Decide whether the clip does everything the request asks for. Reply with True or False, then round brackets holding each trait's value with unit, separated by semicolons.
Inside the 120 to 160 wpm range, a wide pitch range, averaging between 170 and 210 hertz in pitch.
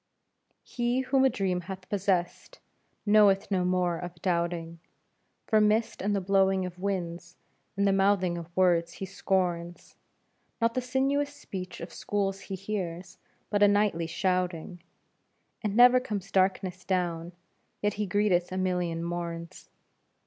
False (140 wpm; 2.8 semitones; 185 Hz)